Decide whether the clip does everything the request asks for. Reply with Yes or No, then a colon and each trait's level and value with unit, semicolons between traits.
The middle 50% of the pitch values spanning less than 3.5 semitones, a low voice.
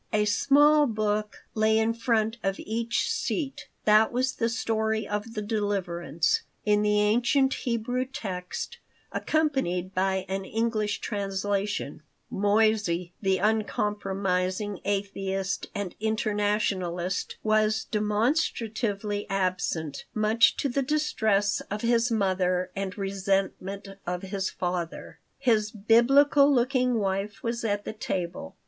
No: average, 2.8 semitones; high, 210 Hz